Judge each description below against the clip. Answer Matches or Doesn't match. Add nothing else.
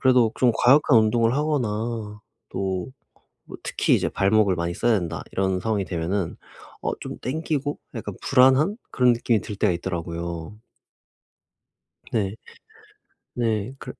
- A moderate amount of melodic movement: Matches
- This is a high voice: Doesn't match